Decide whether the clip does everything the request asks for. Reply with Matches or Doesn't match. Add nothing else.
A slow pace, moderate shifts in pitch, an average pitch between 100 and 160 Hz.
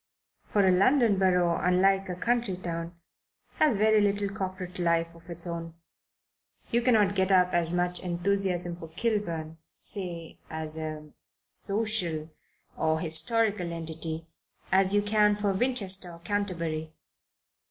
Doesn't match